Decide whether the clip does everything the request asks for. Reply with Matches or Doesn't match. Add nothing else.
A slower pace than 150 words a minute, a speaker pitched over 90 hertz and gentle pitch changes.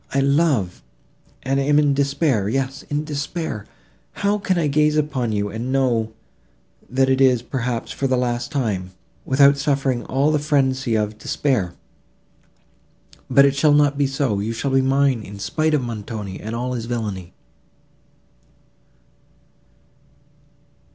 Doesn't match